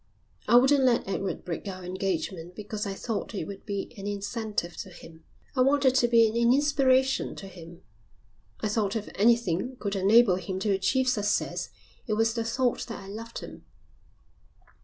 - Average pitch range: Yes, average, 3.8 semitones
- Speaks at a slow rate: No, average, 175 wpm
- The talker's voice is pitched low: No, high, 210 Hz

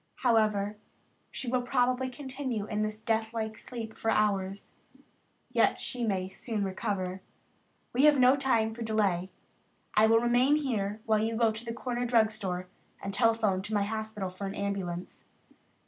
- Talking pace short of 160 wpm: No, average, 165 wpm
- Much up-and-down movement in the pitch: No, average, 3.1 semitones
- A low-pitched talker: No, high, 220 Hz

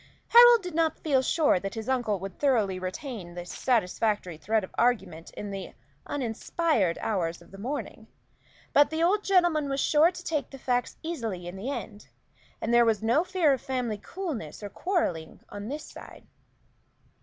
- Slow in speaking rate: No, average, 175 wpm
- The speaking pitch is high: Yes, high, 240 Hz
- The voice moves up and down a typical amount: No, wide, 7.7 semitones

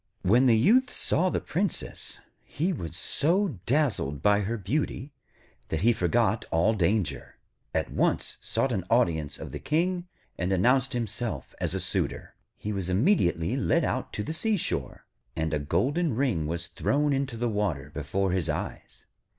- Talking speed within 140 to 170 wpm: Yes, average, 160 wpm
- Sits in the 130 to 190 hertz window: No, low, 110 Hz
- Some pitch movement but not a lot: No, wide, 8.4 semitones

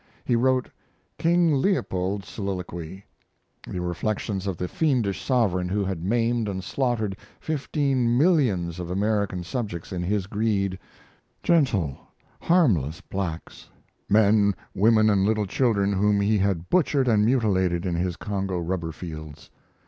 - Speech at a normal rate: No, slow, 130 wpm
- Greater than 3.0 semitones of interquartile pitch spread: Yes, average, 4.4 semitones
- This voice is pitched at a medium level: No, low, 100 Hz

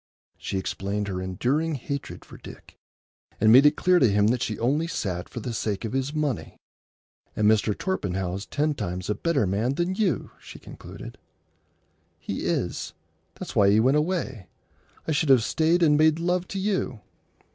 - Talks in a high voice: No, low, 130 Hz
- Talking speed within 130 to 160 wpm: No, average, 175 wpm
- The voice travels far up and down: Yes, wide, 7.4 semitones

